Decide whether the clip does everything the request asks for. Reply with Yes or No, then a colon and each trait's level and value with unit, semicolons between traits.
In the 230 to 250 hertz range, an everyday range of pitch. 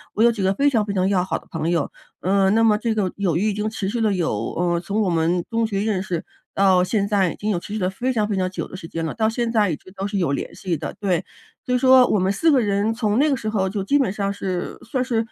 No: high, 200 Hz; average, 3.2 semitones